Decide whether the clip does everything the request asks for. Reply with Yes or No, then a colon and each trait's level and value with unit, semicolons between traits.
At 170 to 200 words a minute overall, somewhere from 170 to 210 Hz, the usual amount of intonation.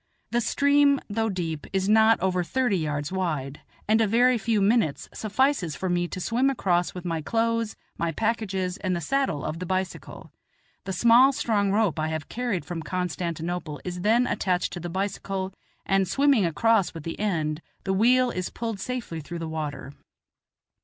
Yes: average, 175 wpm; high, 190 Hz; average, 5.0 semitones